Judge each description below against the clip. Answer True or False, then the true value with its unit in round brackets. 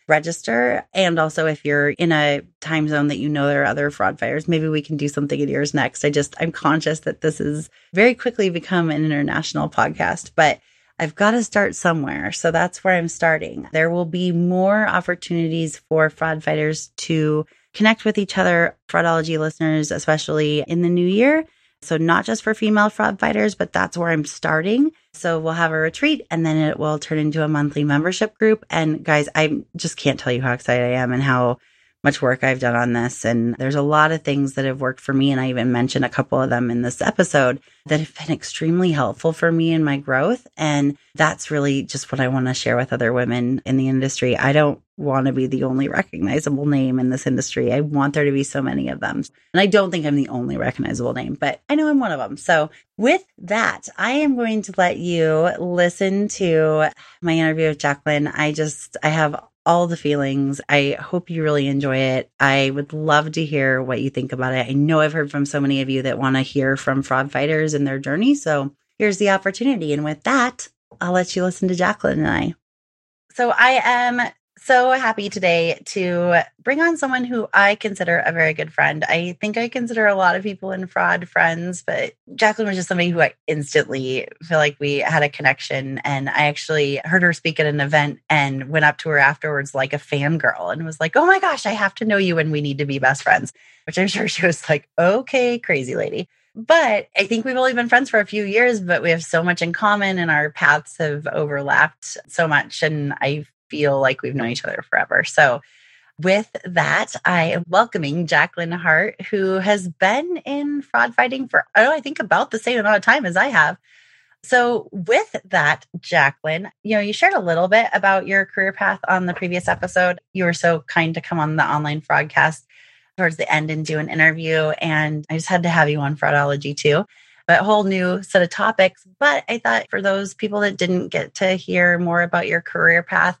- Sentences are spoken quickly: True (220 wpm)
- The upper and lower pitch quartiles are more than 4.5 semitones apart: True (4.9 semitones)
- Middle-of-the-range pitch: True (160 Hz)